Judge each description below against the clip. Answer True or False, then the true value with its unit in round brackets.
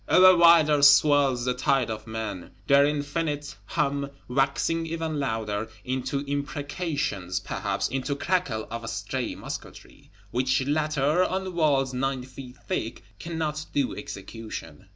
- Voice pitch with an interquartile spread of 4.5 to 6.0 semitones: False (3.9 semitones)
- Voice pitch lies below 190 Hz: True (140 Hz)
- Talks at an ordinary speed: False (125 wpm)